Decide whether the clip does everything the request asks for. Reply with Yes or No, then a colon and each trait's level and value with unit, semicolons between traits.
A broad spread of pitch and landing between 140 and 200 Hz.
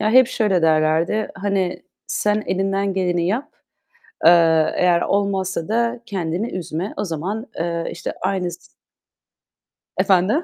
No: average, 3.4 semitones; high, 190 Hz